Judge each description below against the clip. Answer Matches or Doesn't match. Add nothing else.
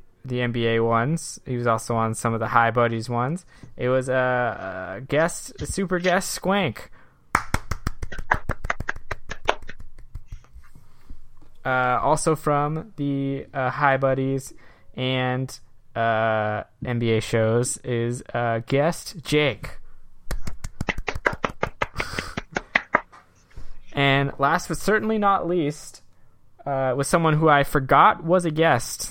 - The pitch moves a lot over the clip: Doesn't match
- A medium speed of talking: Doesn't match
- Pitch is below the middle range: Matches